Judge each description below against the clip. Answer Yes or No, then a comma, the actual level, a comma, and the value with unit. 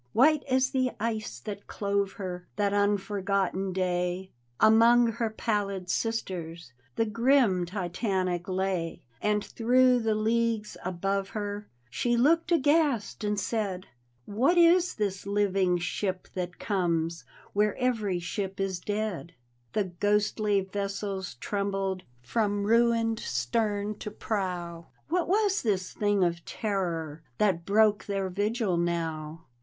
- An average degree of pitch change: Yes, average, 3.5 semitones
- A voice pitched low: No, high, 200 Hz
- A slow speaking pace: Yes, slow, 130 wpm